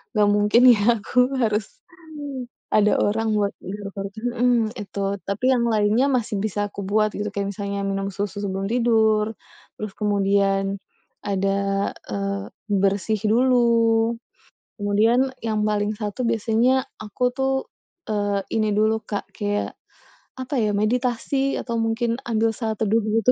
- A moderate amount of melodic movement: No, narrow, 2.3 semitones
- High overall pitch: Yes, high, 215 Hz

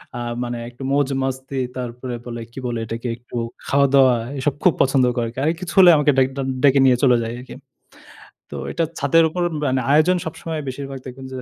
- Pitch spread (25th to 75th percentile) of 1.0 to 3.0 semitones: Yes, narrow, 2.4 semitones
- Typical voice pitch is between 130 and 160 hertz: Yes, low, 135 Hz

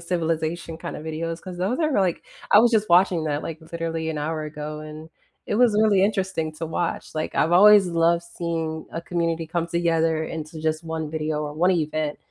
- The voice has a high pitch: No, medium, 165 Hz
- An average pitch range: No, narrow, 1.9 semitones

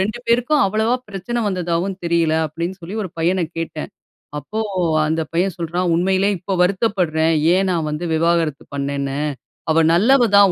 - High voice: No, medium, 175 Hz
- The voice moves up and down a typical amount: Yes, average, 3.3 semitones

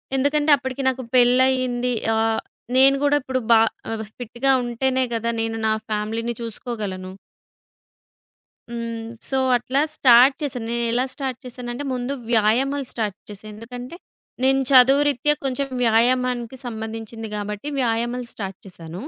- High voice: Yes, high, 240 Hz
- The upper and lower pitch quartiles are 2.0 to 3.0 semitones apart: Yes, narrow, 2.6 semitones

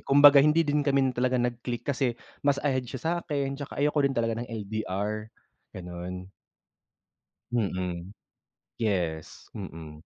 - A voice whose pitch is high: No, low, 120 Hz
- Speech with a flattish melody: No, wide, 6.5 semitones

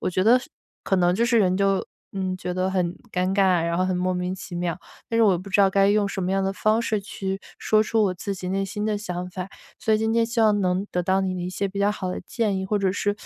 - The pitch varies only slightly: Yes, narrow, 2.2 semitones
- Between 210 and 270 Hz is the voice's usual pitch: No, high, 195 Hz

